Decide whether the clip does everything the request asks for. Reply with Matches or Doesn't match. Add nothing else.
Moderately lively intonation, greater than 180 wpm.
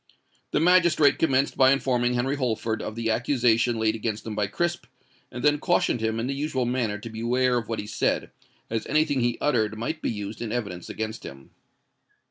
Matches